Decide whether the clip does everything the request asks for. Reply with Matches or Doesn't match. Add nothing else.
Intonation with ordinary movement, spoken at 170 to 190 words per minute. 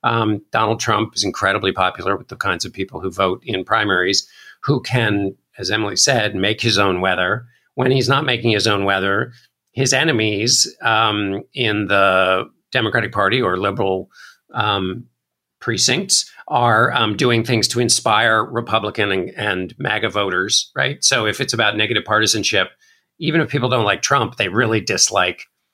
Doesn't match